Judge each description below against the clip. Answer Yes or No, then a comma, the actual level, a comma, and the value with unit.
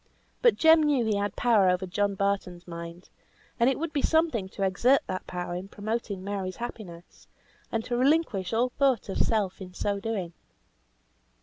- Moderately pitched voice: No, high, 205 Hz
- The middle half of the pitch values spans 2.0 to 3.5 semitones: No, average, 4.6 semitones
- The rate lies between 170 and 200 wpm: Yes, average, 175 wpm